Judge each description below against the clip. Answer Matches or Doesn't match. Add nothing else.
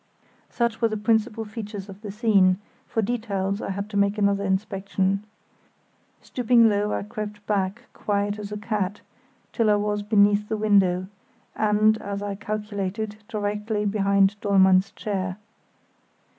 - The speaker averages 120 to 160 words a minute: Matches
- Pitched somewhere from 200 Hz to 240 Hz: Matches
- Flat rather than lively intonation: Matches